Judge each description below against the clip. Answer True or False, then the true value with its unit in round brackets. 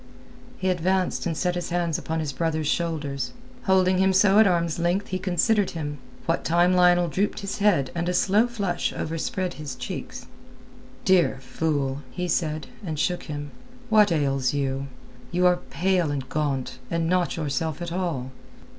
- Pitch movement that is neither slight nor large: True (3.6 semitones)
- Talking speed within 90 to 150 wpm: False (165 wpm)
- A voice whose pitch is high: False (170 Hz)